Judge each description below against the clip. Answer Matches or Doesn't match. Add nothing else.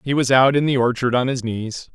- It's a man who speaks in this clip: Matches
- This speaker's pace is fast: Matches